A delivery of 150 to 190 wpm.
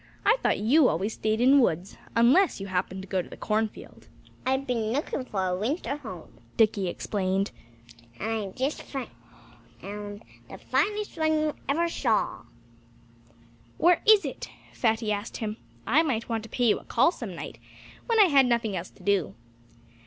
Yes: average, 175 wpm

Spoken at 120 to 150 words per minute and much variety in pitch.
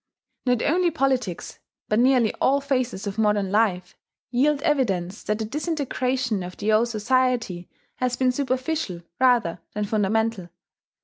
No: slow, 135 wpm; average, 4.0 semitones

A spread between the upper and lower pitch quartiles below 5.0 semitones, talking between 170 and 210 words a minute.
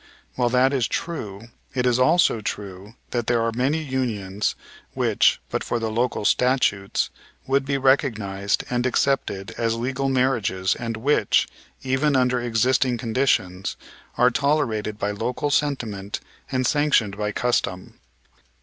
No: average, 3.9 semitones; slow, 135 wpm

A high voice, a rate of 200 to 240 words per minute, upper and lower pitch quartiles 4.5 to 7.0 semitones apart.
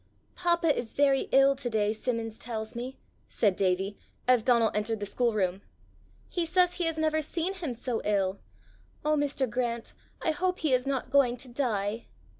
No: very high, 250 Hz; average, 175 wpm; wide, 5.6 semitones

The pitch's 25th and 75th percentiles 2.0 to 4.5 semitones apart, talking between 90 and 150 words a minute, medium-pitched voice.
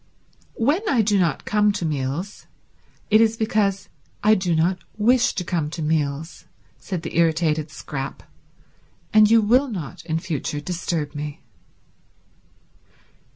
No: wide, 5.4 semitones; slow, 135 wpm; medium, 175 Hz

